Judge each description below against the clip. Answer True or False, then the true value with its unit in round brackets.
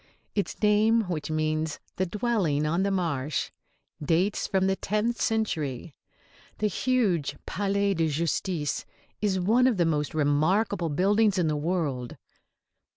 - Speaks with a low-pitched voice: False (180 Hz)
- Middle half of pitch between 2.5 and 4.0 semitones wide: False (4.9 semitones)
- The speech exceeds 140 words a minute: False (135 wpm)